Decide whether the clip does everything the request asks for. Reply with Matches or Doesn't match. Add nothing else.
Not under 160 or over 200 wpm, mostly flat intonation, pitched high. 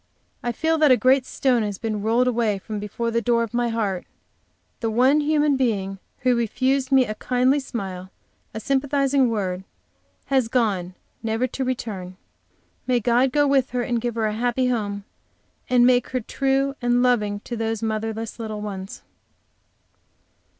Doesn't match